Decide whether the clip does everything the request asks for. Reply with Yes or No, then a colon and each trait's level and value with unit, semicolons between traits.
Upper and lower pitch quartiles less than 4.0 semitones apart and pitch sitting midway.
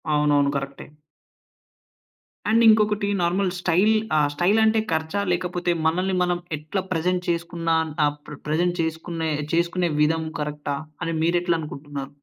Yes: average, 3.2 semitones; medium, 170 Hz